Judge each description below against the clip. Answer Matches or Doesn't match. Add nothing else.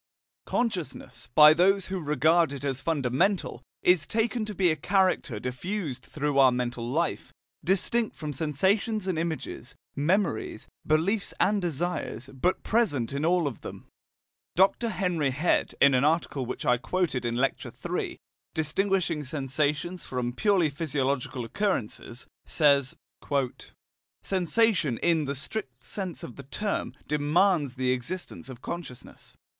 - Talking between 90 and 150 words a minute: Matches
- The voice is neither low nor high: Matches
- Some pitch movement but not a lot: Doesn't match